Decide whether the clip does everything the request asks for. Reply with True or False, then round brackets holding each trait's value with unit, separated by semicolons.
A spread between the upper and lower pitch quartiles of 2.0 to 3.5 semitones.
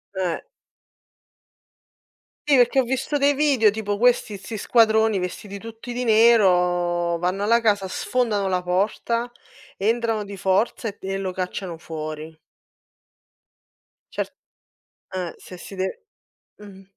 False (4.0 semitones)